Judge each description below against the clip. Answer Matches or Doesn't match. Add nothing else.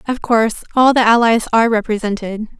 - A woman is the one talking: Matches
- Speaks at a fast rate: Doesn't match